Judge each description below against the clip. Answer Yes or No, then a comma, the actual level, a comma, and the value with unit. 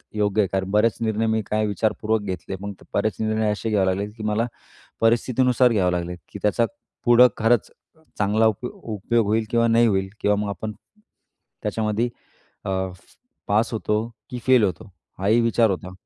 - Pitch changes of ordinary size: No, narrow, 2.0 semitones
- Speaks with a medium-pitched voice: No, low, 110 Hz